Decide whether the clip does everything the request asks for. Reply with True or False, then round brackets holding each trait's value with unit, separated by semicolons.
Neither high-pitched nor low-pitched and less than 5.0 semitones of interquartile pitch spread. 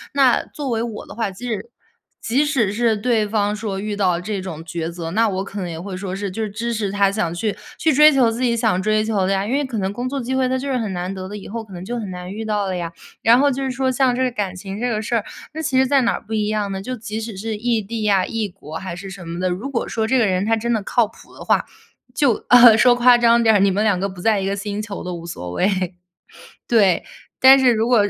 False (215 Hz; 3.6 semitones)